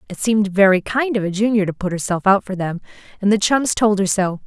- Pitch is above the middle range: Yes, high, 200 Hz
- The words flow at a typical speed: No, fast, 255 wpm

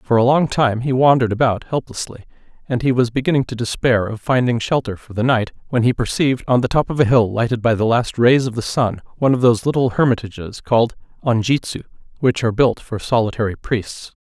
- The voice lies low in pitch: Yes, low, 120 Hz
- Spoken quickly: Yes, fast, 210 wpm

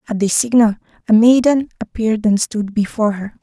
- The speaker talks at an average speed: Yes, average, 175 wpm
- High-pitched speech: Yes, high, 220 Hz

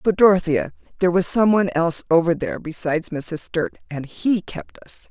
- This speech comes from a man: No, female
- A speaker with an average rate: Yes, average, 190 wpm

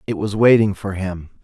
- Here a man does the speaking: Yes, male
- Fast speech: Yes, fast, 210 wpm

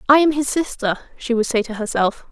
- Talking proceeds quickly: Yes, fast, 235 wpm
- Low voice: No, high, 245 Hz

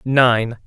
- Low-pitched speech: Yes, low, 120 Hz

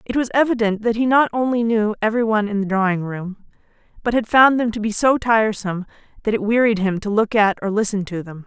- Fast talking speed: Yes, fast, 225 wpm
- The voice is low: No, high, 215 Hz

